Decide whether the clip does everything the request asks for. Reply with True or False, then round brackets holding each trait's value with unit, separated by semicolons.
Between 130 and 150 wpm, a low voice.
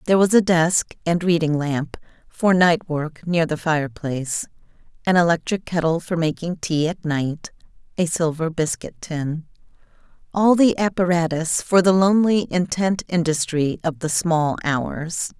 False (145 wpm; 165 Hz)